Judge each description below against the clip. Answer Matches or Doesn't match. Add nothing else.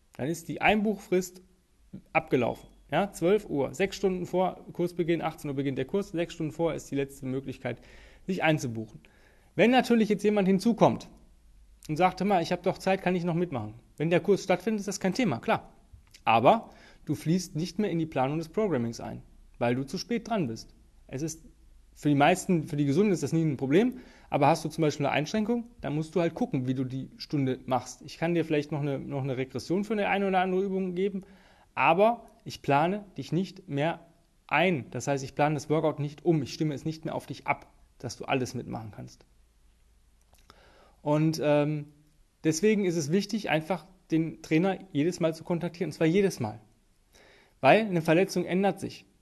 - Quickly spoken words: Matches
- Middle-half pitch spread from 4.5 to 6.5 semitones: Matches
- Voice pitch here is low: Doesn't match